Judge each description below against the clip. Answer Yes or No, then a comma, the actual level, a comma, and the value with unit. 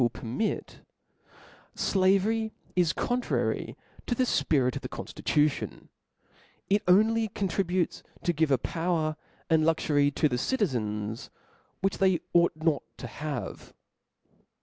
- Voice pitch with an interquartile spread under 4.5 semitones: No, wide, 5.4 semitones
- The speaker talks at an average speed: No, slow, 120 wpm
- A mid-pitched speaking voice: Yes, medium, 165 Hz